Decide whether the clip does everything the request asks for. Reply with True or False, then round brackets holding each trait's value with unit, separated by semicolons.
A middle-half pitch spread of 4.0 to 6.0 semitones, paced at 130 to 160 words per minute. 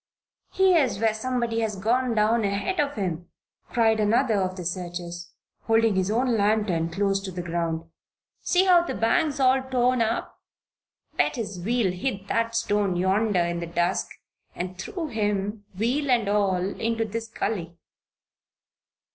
True (4.3 semitones; 150 wpm)